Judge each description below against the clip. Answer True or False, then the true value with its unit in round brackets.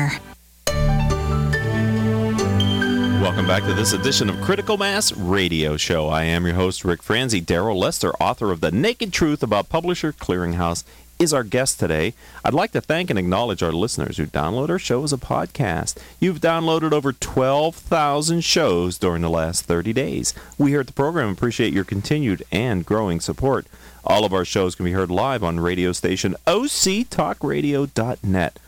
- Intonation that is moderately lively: False (8.4 semitones)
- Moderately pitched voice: False (105 Hz)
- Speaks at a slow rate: False (165 wpm)